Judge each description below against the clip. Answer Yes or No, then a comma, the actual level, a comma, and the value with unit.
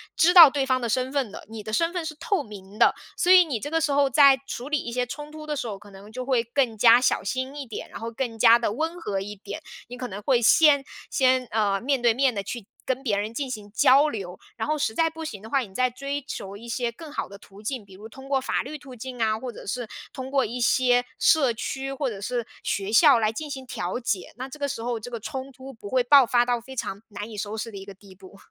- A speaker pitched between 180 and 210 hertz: No, high, 245 Hz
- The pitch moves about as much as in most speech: Yes, average, 4.0 semitones